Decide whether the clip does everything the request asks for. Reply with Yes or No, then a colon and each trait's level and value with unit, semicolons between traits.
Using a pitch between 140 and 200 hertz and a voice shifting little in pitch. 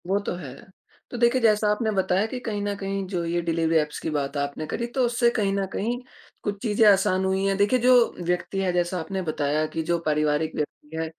No: high, 190 Hz; average, 4.6 semitones